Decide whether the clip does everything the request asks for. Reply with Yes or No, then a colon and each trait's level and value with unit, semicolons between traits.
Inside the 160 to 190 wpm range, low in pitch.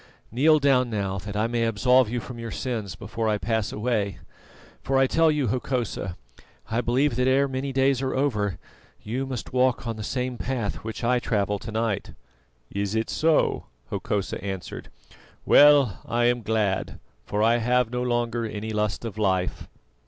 Yes: average, 175 wpm; low, 115 Hz